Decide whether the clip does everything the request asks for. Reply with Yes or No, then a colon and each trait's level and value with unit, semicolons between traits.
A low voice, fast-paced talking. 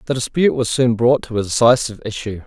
Yes: low, 120 Hz; fast, 220 wpm